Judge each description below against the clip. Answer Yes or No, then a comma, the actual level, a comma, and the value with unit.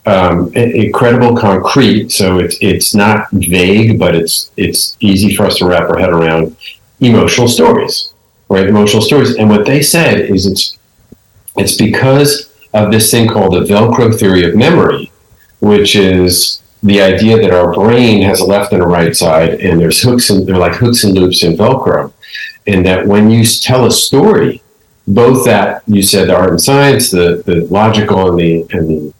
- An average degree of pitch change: Yes, average, 3.8 semitones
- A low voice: Yes, low, 105 Hz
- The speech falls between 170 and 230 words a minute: Yes, average, 180 wpm